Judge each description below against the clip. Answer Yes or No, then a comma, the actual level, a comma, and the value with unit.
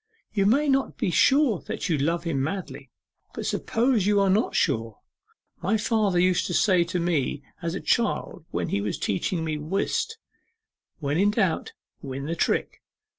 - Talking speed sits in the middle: Yes, average, 175 wpm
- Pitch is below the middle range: No, medium, 180 Hz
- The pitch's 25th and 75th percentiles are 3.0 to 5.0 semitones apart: No, wide, 5.6 semitones